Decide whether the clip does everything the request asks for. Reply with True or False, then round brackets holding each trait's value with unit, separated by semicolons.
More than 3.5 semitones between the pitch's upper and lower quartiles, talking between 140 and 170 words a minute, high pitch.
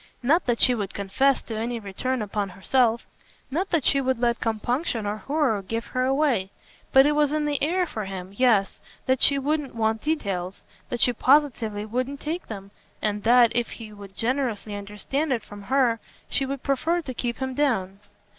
False (4.7 semitones; 190 wpm; 240 Hz)